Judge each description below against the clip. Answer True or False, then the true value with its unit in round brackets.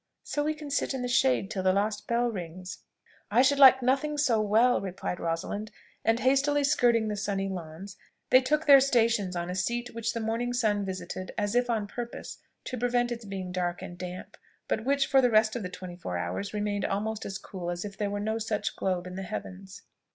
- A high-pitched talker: True (215 Hz)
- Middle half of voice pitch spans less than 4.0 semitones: False (4.6 semitones)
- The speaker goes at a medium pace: False (215 wpm)